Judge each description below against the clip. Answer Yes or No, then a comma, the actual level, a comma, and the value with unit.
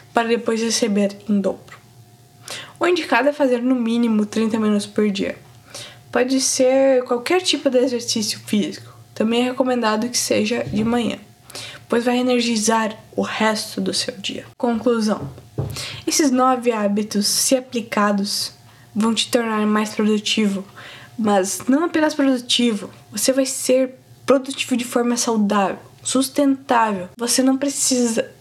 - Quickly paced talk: No, average, 135 wpm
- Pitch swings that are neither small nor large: Yes, average, 3.6 semitones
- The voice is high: Yes, high, 235 Hz